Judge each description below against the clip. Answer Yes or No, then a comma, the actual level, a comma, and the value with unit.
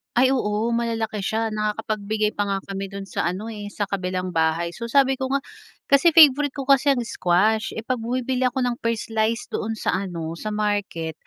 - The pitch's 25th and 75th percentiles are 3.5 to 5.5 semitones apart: Yes, average, 3.9 semitones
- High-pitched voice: Yes, high, 220 Hz